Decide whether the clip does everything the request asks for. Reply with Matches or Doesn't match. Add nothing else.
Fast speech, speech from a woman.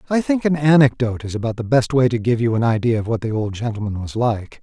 Doesn't match